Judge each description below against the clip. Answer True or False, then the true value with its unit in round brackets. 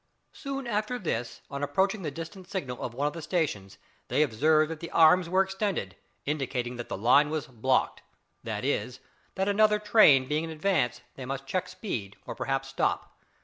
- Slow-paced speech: False (185 wpm)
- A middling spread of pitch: False (6.5 semitones)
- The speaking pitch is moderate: True (155 Hz)